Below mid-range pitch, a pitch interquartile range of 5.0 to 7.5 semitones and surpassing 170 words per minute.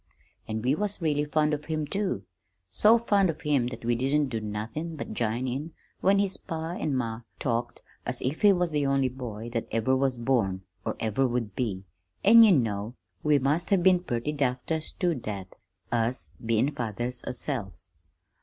Yes: low, 130 Hz; average, 5.3 semitones; average, 185 wpm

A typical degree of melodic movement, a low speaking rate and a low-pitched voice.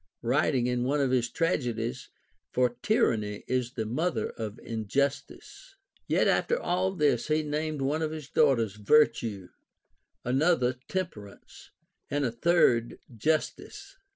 Yes: average, 4.9 semitones; slow, 130 wpm; low, 130 Hz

